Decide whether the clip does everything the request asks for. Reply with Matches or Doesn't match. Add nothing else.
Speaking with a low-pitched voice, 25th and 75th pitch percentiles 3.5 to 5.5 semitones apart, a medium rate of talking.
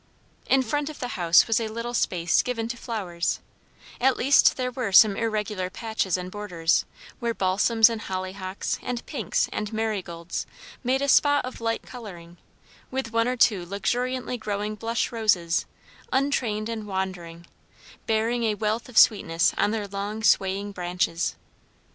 Doesn't match